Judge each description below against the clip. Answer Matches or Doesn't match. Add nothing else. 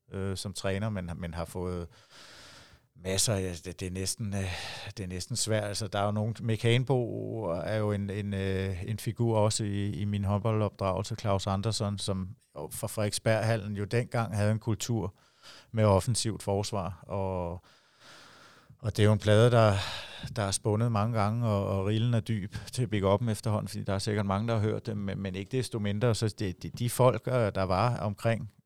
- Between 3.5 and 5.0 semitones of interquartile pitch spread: Doesn't match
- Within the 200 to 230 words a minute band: Doesn't match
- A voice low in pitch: Matches